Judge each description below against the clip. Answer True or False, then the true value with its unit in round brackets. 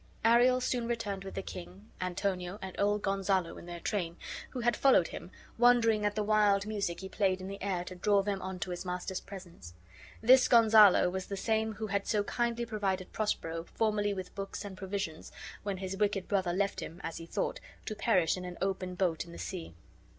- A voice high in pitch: True (195 Hz)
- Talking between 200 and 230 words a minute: True (205 wpm)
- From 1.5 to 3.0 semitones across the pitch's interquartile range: True (2.6 semitones)